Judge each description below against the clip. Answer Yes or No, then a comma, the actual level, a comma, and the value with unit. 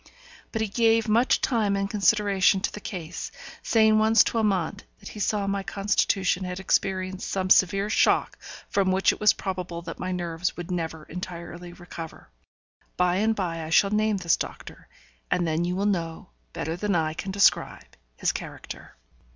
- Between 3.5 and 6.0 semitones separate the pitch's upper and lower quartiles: No, average, 2.9 semitones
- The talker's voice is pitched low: No, high, 190 Hz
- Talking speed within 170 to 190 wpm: Yes, average, 175 wpm